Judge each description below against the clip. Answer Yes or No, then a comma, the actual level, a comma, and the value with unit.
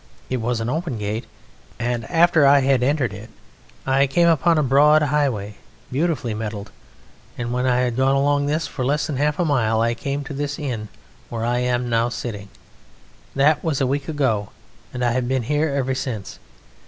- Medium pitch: No, low, 130 Hz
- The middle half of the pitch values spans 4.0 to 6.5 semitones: No, average, 3.6 semitones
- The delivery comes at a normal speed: Yes, average, 190 wpm